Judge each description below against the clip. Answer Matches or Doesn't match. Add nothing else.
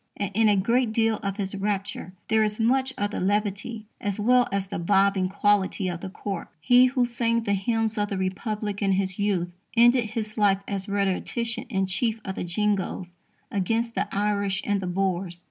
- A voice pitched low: Doesn't match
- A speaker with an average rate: Matches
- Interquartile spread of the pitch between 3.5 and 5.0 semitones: Doesn't match